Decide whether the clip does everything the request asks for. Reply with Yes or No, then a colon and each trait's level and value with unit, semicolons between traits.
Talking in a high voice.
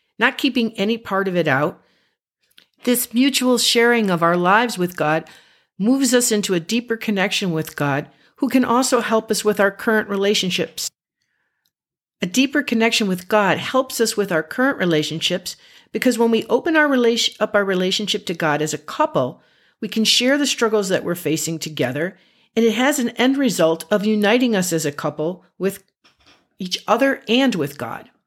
Yes: high, 215 Hz